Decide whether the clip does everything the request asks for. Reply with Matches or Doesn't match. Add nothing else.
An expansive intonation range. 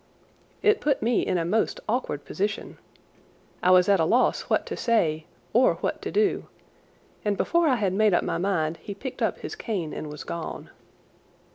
Matches